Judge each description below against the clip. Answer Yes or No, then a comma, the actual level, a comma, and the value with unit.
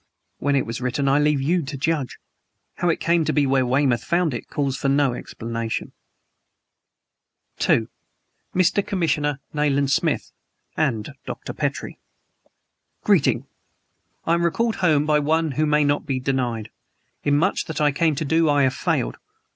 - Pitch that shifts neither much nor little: Yes, average, 3.1 semitones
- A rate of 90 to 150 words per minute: No, average, 160 wpm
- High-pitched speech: No, medium, 145 Hz